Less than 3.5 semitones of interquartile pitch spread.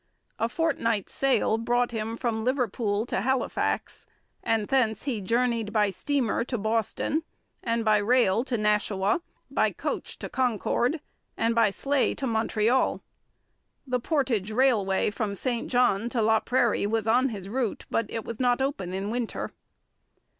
Yes: average, 2.9 semitones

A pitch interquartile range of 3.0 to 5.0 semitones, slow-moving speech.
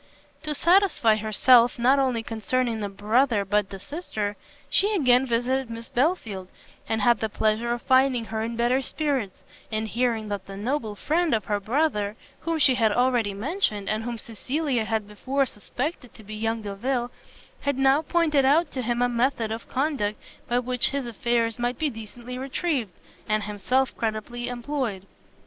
No: average, 3.6 semitones; average, 170 wpm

